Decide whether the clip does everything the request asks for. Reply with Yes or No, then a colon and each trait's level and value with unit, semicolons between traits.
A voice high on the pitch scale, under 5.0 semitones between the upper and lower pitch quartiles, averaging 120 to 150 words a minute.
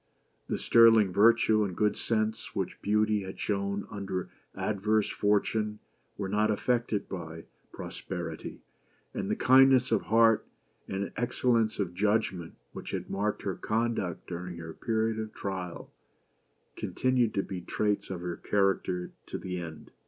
No: low, 105 Hz; average, 2.8 semitones; average, 145 wpm